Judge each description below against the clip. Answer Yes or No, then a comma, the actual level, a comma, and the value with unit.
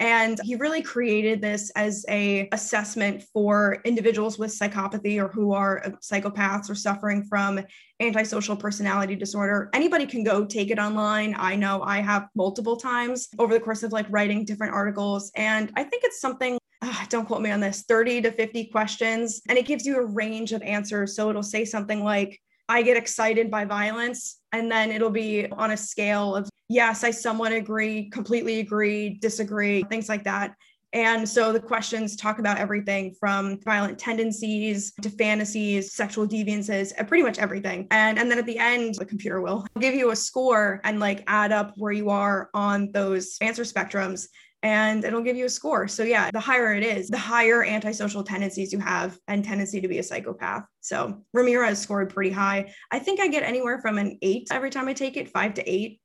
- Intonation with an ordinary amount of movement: No, narrow, 2.1 semitones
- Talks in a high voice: Yes, high, 215 Hz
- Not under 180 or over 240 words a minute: Yes, average, 195 wpm